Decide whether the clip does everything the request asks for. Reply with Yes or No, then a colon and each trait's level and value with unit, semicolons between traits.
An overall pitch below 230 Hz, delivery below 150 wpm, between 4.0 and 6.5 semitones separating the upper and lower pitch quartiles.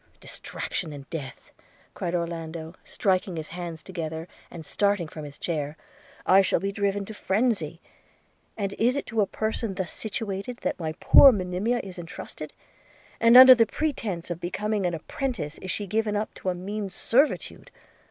No: high, 190 Hz; average, 170 wpm; average, 4.5 semitones